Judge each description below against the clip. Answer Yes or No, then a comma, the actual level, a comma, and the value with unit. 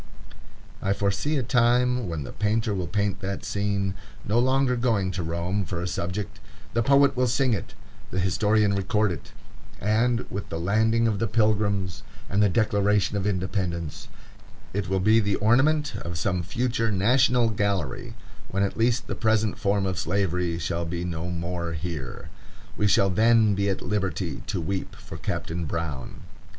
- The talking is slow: No, average, 165 wpm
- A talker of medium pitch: No, low, 100 Hz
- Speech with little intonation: No, average, 3.8 semitones